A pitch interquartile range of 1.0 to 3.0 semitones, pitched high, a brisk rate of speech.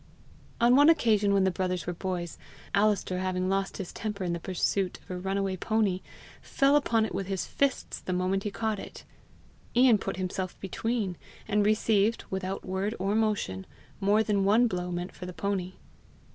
No: average, 2.7 semitones; high, 195 Hz; average, 180 wpm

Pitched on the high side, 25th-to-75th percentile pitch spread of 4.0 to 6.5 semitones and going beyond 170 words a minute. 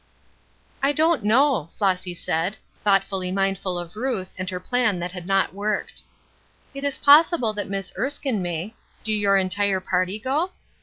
No: high, 200 Hz; average, 5.2 semitones; average, 155 wpm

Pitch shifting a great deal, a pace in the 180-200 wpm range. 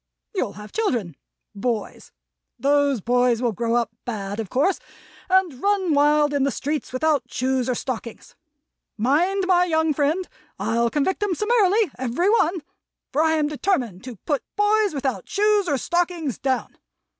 No: wide, 6.7 semitones; average, 155 wpm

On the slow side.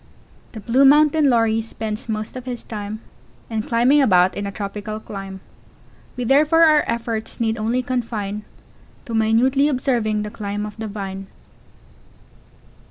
No: average, 150 wpm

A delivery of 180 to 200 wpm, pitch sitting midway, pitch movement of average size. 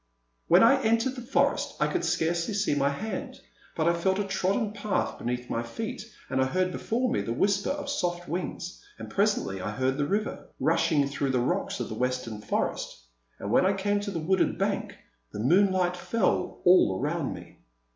No: average, 190 wpm; medium, 180 Hz; wide, 7.0 semitones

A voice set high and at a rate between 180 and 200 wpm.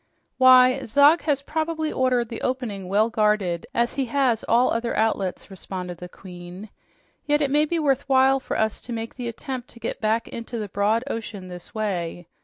Yes: high, 230 Hz; average, 195 wpm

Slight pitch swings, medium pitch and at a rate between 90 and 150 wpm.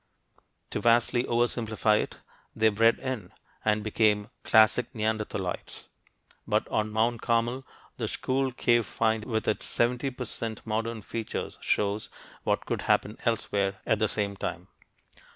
No: narrow, 1.8 semitones; low, 110 Hz; average, 140 wpm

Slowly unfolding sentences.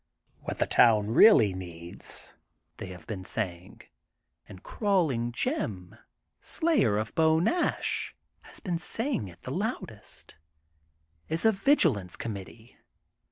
Yes: slow, 125 wpm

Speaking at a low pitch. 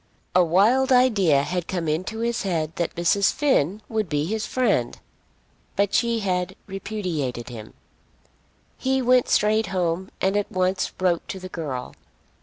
No: high, 190 Hz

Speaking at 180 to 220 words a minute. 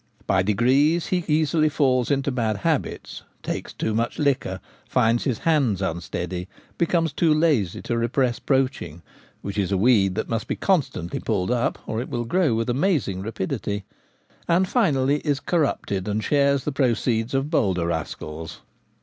No: average, 160 wpm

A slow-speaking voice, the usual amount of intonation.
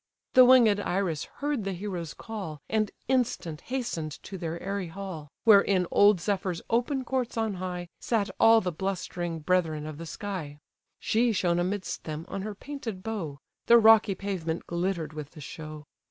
No: average, 170 wpm; average, 4.8 semitones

